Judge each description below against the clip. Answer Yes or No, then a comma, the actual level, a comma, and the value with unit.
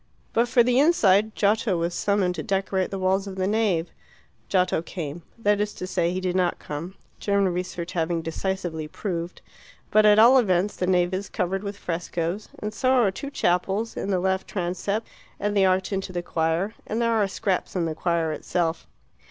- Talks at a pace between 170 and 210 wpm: Yes, average, 195 wpm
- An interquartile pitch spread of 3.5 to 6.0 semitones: No, average, 2.9 semitones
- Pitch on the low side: No, high, 190 Hz